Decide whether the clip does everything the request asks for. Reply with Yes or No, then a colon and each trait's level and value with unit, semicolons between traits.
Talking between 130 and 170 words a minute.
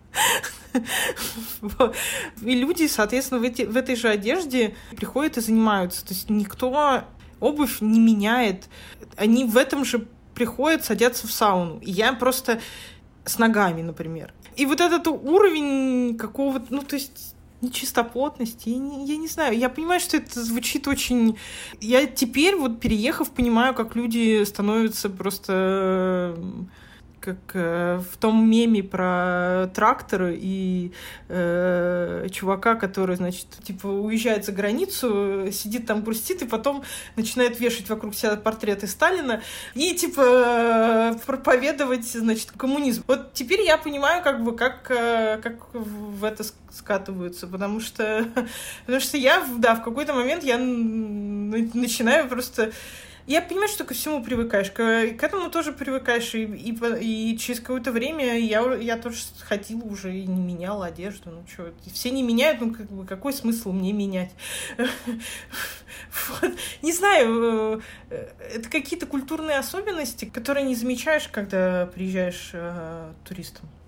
Yes: average, 135 wpm